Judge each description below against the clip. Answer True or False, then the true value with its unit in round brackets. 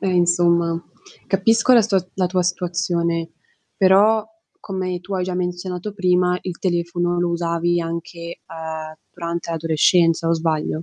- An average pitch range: False (1.6 semitones)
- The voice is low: False (175 Hz)